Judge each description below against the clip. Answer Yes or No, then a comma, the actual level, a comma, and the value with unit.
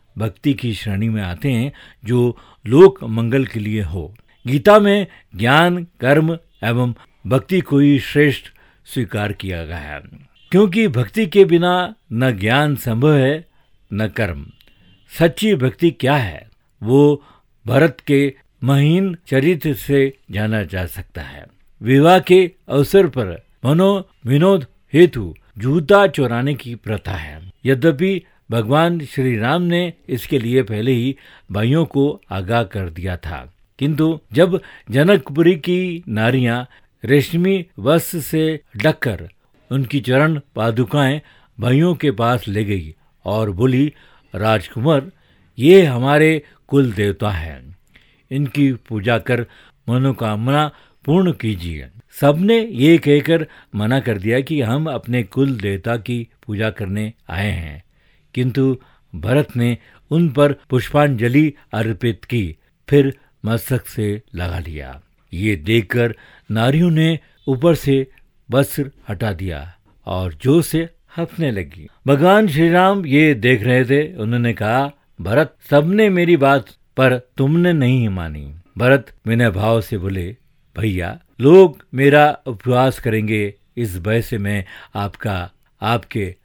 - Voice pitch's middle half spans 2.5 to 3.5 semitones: No, wide, 5.6 semitones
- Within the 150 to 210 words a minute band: No, average, 125 wpm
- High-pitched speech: No, low, 130 Hz